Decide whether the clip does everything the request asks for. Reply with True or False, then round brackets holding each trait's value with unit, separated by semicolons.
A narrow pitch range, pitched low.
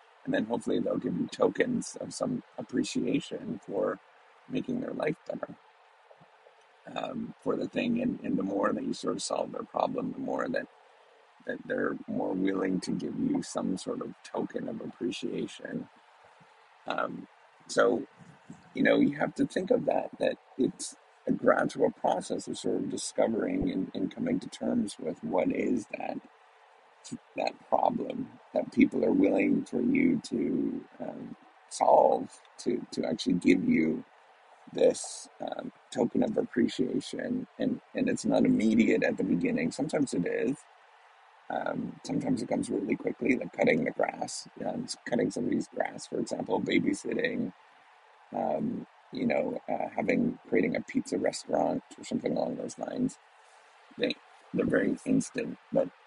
False (2.2 semitones; 260 Hz)